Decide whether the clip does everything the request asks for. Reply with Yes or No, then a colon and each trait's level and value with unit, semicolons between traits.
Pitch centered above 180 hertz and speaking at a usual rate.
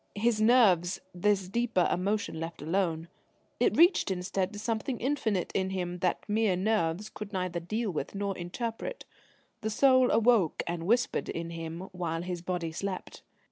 Yes: high, 190 Hz; average, 155 wpm